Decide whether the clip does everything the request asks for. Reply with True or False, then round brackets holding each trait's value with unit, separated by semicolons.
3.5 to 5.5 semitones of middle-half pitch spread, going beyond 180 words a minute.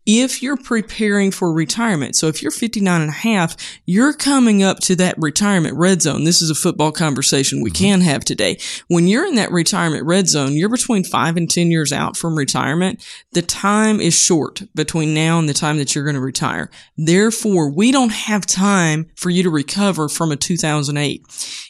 True (4.6 semitones; 195 wpm)